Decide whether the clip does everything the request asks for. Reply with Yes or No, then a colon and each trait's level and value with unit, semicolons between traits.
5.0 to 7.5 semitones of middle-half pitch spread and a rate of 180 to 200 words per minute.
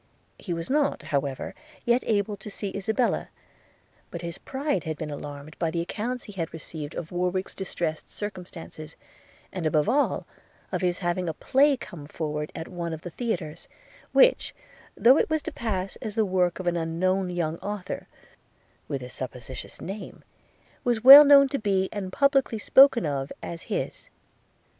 No: wide, 5.5 semitones; average, 165 wpm